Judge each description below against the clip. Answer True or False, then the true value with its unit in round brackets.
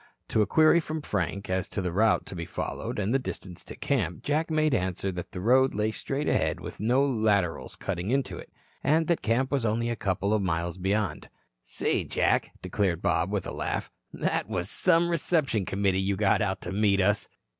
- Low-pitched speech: True (105 Hz)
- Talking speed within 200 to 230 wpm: True (205 wpm)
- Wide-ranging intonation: True (6.0 semitones)